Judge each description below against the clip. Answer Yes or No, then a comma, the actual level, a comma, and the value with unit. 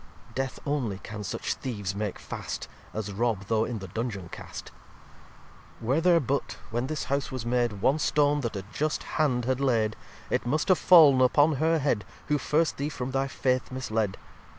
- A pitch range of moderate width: Yes, average, 4.9 semitones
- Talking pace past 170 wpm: Yes, average, 185 wpm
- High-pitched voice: No, low, 130 Hz